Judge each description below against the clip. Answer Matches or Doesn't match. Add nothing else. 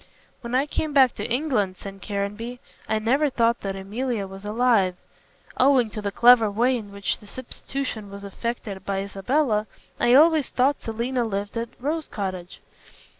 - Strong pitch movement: Doesn't match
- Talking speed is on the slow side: Doesn't match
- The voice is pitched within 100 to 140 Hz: Doesn't match